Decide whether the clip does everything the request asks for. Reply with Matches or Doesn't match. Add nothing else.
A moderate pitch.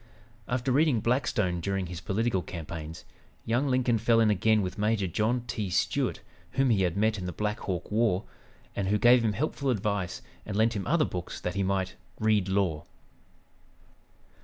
Doesn't match